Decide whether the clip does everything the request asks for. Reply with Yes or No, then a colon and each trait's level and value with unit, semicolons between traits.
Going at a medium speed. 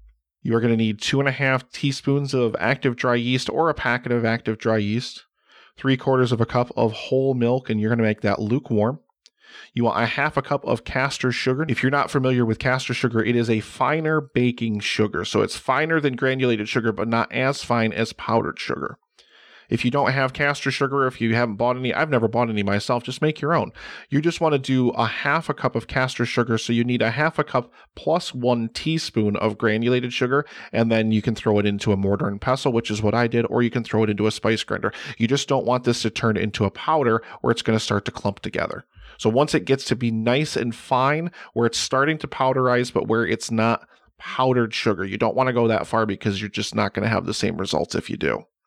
No: fast, 245 wpm